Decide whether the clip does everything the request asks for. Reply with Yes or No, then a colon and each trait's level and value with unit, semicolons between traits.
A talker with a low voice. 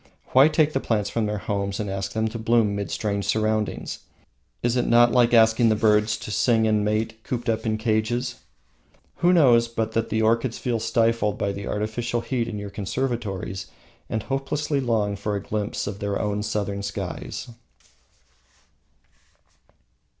Yes: low, 110 Hz